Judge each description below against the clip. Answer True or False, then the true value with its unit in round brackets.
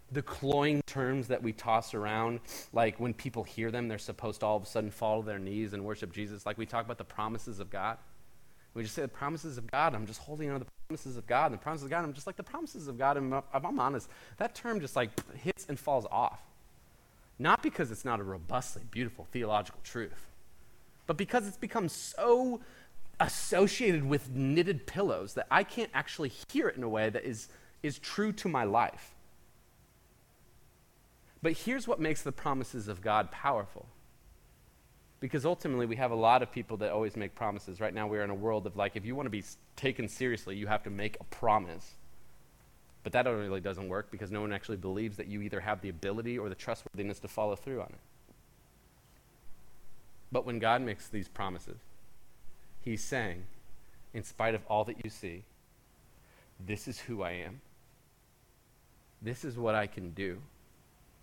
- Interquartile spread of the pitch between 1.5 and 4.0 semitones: False (4.9 semitones)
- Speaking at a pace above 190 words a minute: True (200 wpm)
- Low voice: True (115 Hz)